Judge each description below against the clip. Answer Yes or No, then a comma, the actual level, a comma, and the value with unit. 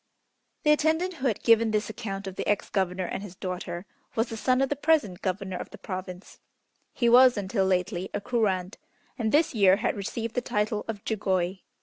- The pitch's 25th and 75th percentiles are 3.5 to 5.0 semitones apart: Yes, average, 3.9 semitones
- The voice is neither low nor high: No, high, 210 Hz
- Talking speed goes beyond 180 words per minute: Yes, average, 200 wpm